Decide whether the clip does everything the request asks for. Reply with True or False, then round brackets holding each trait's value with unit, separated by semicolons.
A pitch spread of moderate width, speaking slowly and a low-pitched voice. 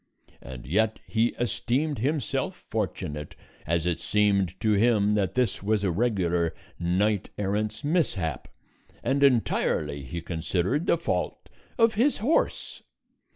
False (6.3 semitones; 125 wpm; 105 Hz)